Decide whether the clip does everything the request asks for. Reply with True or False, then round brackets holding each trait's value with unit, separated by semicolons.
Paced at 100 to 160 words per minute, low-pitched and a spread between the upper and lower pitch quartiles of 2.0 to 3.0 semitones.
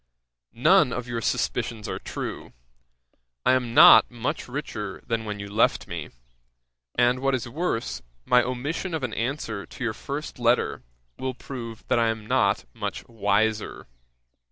True (155 wpm; 120 Hz; 2.6 semitones)